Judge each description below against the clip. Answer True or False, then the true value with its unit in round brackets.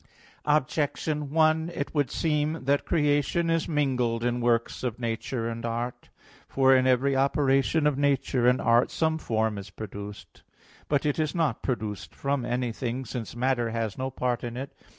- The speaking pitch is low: True (130 Hz)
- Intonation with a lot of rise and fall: False (3.8 semitones)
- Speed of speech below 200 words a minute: True (165 wpm)